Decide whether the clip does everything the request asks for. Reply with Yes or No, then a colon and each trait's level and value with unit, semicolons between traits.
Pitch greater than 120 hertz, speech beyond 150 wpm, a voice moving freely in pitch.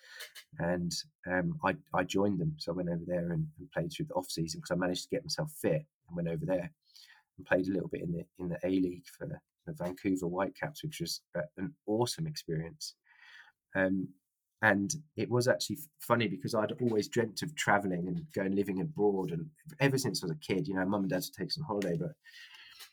No: low, 105 Hz; fast, 205 wpm; wide, 8.7 semitones